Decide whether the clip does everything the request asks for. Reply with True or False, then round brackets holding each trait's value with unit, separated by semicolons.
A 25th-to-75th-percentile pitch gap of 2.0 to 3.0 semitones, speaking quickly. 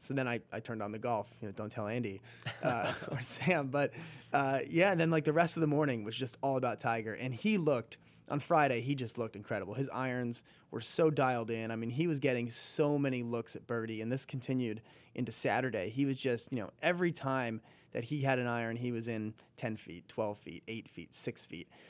False (3.7 semitones; 235 wpm)